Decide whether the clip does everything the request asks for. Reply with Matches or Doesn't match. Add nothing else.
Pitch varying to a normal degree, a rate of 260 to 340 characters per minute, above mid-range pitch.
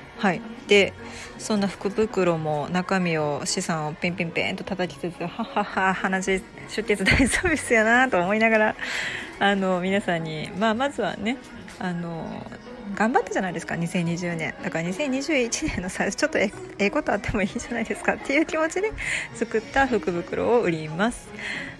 Matches